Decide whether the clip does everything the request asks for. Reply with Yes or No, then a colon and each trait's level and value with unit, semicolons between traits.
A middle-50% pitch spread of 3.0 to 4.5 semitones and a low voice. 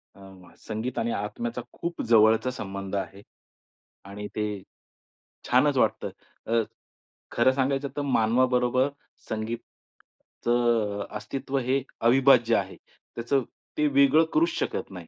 Yes: average, 3.6 semitones; low, 120 Hz